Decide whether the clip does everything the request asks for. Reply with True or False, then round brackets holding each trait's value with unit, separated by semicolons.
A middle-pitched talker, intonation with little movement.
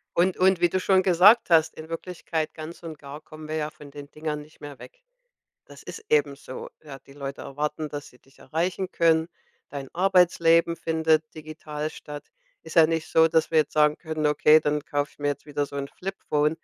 True (155 Hz; 2.2 semitones)